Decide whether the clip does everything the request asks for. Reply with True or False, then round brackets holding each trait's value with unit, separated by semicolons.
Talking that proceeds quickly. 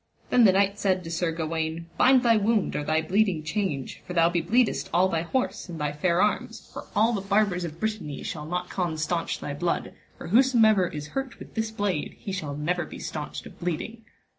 True (215 wpm)